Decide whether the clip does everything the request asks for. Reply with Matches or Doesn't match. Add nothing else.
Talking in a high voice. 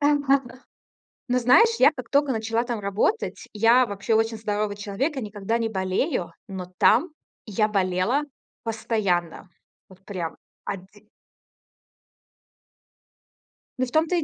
Matches